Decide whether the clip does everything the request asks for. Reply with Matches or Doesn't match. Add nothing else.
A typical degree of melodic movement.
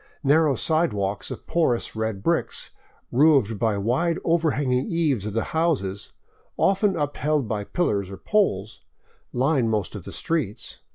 Doesn't match